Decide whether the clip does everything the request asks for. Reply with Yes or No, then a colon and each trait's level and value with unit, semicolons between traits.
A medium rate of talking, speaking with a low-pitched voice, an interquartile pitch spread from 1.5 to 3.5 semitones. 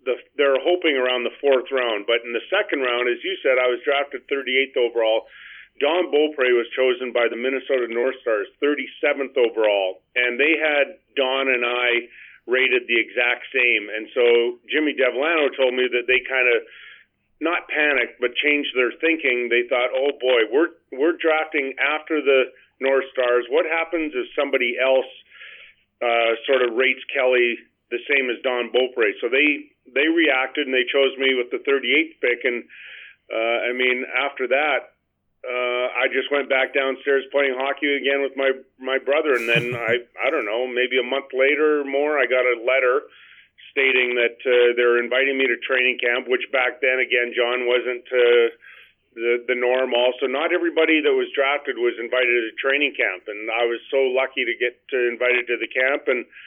Yes: average, 185 wpm; low, 130 Hz; average, 2.8 semitones